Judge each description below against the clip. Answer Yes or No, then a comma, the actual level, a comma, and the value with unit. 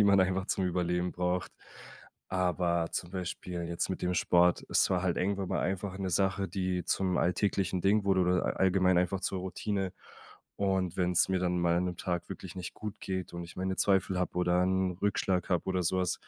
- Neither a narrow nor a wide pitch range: No, narrow, 1.2 semitones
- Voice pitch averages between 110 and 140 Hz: No, very low, 90 Hz